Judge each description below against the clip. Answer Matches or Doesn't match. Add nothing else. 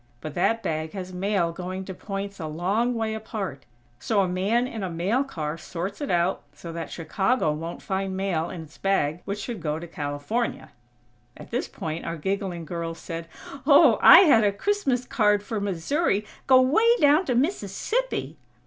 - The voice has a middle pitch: Doesn't match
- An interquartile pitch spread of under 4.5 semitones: Doesn't match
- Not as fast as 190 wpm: Matches